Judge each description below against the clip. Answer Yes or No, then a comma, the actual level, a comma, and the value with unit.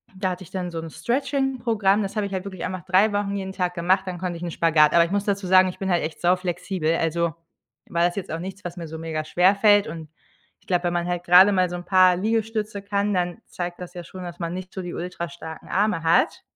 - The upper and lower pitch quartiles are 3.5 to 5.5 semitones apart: No, narrow, 2.5 semitones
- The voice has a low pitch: No, medium, 180 Hz